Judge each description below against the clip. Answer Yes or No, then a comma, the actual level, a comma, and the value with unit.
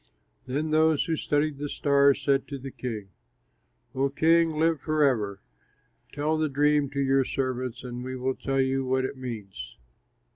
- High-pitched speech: No, low, 135 Hz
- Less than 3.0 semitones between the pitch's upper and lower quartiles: Yes, narrow, 2.5 semitones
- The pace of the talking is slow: No, average, 160 wpm